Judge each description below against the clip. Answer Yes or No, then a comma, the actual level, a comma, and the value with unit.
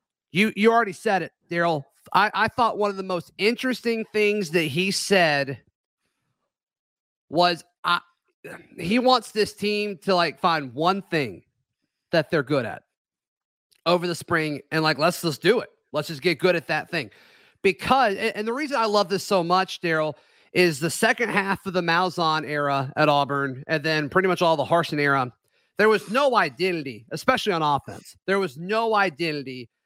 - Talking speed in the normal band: Yes, average, 175 wpm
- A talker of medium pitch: Yes, medium, 175 Hz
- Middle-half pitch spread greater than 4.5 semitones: Yes, average, 4.9 semitones